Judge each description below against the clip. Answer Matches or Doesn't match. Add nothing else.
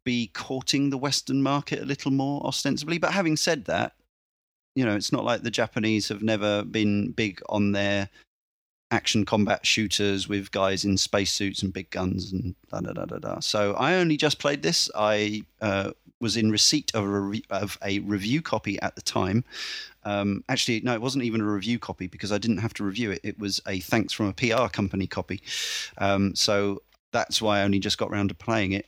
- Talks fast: Matches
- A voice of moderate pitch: Doesn't match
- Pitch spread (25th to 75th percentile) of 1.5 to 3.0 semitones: Doesn't match